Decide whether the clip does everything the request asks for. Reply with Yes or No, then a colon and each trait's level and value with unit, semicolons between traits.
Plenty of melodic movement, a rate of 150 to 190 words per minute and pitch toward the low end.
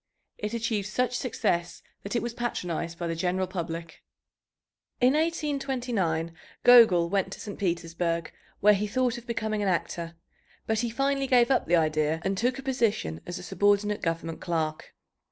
No: wide, 6.1 semitones; average, 165 wpm; high, 200 Hz